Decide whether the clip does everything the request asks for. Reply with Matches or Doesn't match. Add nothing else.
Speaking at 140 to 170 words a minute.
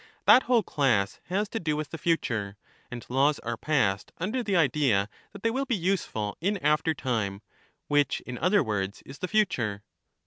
Doesn't match